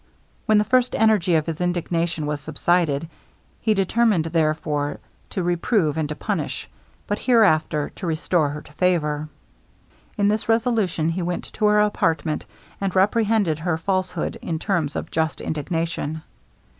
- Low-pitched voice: No, medium, 170 Hz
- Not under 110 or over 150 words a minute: Yes, average, 145 wpm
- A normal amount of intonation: Yes, average, 4.6 semitones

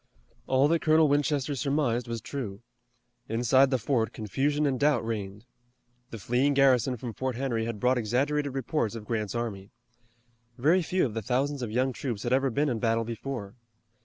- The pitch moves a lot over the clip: No, average, 3.5 semitones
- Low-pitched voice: Yes, low, 125 Hz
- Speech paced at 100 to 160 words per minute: No, average, 175 wpm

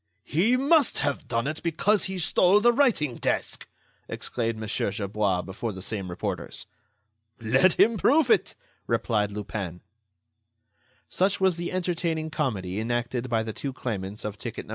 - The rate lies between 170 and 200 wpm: No, average, 150 wpm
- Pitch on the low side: Yes, low, 125 Hz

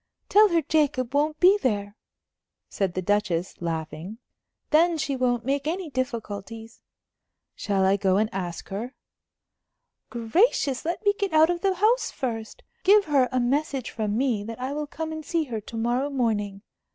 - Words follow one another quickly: No, average, 165 wpm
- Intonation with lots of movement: Yes, wide, 7.1 semitones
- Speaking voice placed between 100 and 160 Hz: No, very high, 255 Hz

